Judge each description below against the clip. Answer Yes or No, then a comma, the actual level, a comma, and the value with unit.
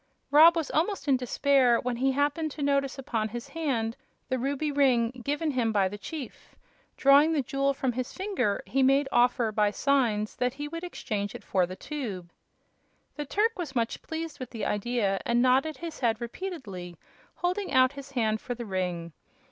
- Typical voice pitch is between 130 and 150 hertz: No, very high, 260 Hz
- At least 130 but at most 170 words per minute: No, average, 185 wpm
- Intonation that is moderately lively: Yes, average, 4.4 semitones